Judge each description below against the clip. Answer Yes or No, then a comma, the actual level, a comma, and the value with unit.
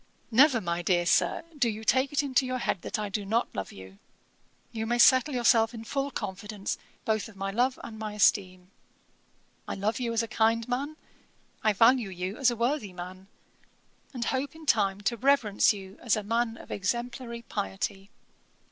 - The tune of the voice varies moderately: Yes, average, 3.9 semitones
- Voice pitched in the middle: No, high, 225 Hz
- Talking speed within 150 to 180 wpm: No, average, 190 wpm